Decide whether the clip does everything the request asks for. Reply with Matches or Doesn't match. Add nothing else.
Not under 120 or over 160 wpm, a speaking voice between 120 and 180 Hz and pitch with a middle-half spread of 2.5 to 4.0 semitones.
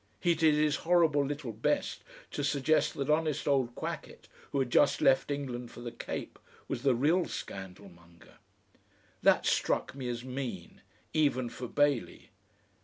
Matches